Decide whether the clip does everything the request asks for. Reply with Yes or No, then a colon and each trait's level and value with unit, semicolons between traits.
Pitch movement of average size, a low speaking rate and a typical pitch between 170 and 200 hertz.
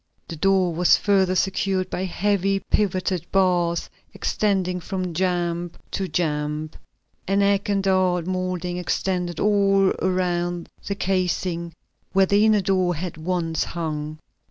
No: narrow, 2.0 semitones; slow, 130 wpm; medium, 185 Hz